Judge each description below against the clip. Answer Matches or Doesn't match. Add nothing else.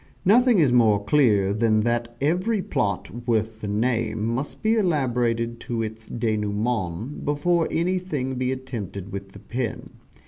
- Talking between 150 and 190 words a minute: Doesn't match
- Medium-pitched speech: Doesn't match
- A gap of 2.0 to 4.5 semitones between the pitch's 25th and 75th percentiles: Doesn't match